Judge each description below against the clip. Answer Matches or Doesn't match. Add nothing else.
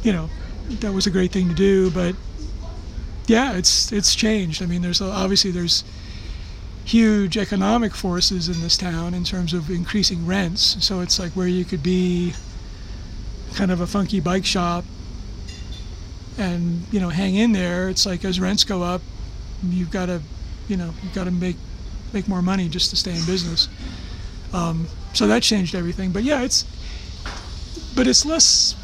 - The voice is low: Doesn't match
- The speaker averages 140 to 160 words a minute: Doesn't match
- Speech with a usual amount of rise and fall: Matches